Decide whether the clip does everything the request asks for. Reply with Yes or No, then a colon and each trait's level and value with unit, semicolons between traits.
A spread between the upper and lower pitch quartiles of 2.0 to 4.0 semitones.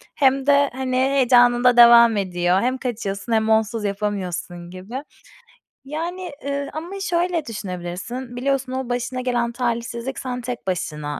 No: average, 4.4 semitones